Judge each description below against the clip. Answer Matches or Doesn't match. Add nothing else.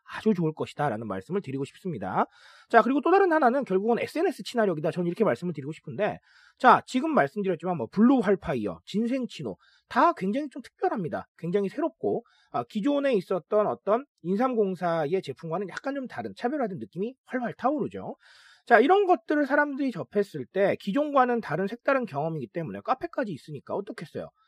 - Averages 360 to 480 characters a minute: Matches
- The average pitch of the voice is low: Doesn't match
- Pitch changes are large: Matches